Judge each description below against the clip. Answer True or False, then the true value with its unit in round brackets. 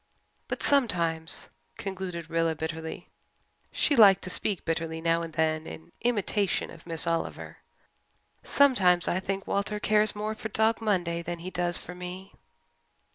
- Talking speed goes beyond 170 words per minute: False (145 wpm)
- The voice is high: False (180 Hz)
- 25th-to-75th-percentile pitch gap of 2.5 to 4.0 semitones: True (3.7 semitones)